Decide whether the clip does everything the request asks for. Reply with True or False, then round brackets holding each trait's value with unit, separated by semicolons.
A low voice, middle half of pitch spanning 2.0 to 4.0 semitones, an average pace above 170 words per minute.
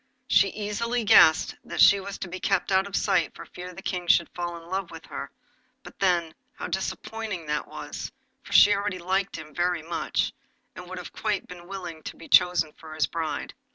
False (180 Hz; 2.8 semitones; 205 wpm)